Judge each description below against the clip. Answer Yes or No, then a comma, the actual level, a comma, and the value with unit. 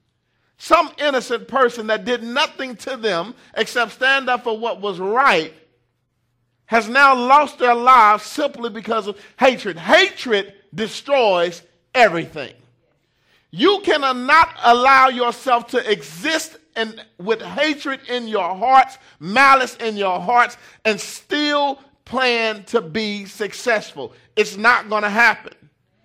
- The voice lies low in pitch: No, high, 230 Hz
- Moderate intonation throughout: Yes, average, 4.5 semitones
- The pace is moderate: No, slow, 125 wpm